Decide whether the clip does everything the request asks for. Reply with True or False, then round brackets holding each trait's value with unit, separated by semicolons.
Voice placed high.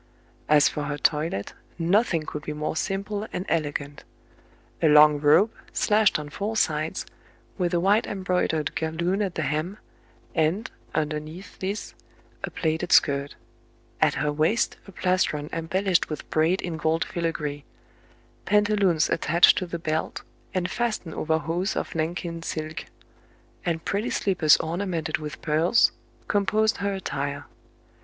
False (165 Hz)